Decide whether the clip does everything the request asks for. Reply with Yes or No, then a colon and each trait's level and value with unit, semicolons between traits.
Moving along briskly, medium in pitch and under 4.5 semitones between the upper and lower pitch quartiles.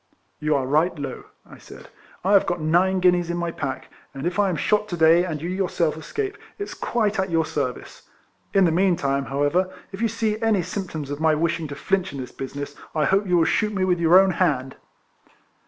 Yes: fast, 230 wpm; medium, 170 Hz; average, 4.0 semitones